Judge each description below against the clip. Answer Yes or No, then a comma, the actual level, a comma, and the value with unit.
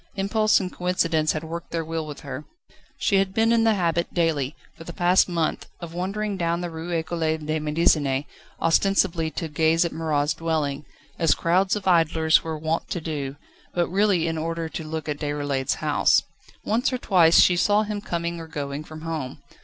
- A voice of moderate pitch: Yes, medium, 165 Hz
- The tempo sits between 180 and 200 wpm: Yes, average, 190 wpm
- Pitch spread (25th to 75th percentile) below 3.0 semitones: Yes, narrow, 2.4 semitones